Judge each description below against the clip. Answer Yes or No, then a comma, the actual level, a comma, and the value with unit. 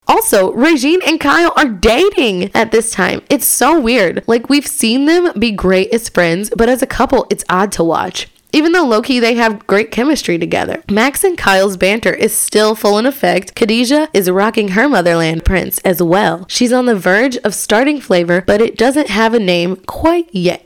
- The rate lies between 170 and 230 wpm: Yes, average, 200 wpm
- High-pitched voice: Yes, high, 225 Hz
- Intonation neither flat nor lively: No, wide, 6.1 semitones